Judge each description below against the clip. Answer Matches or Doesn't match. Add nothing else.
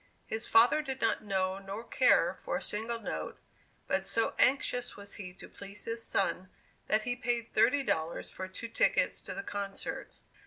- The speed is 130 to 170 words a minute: Doesn't match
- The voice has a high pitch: Matches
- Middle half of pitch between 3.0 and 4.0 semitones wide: Matches